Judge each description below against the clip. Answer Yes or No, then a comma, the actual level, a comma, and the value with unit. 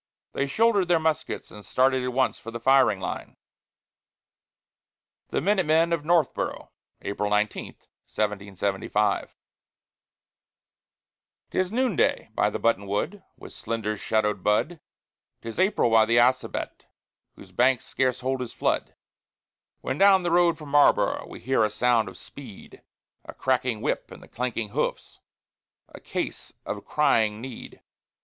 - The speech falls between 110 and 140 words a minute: Yes, slow, 135 wpm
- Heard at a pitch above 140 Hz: No, low, 125 Hz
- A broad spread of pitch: Yes, wide, 6.5 semitones